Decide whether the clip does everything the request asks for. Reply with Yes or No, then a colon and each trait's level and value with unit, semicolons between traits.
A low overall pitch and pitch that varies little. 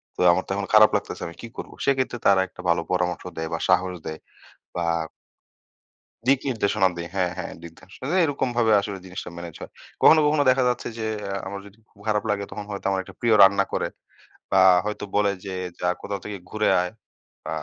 No: low, 100 Hz; average, 3.3 semitones